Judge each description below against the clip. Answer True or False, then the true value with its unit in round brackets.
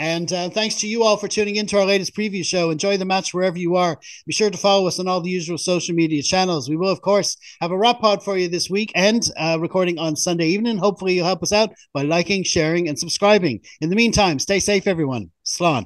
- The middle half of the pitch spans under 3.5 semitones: True (3.1 semitones)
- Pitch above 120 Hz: True (185 Hz)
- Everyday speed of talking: False (255 wpm)